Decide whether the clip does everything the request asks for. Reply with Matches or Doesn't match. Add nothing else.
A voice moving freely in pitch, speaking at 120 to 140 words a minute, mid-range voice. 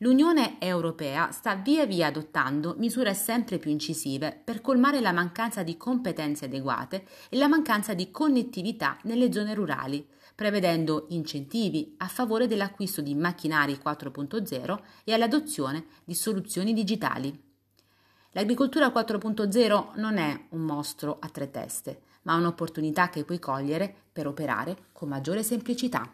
Matches